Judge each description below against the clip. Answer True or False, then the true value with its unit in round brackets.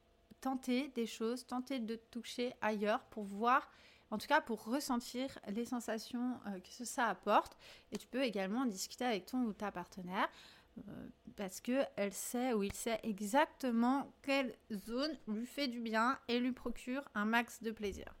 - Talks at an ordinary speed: True (170 wpm)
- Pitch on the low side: False (235 Hz)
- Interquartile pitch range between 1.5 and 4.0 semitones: True (2.8 semitones)